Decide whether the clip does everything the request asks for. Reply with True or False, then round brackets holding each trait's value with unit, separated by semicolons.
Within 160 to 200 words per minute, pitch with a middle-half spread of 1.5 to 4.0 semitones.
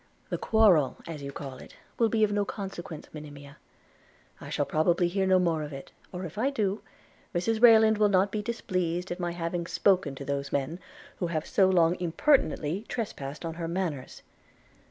False (190 wpm; 4.7 semitones)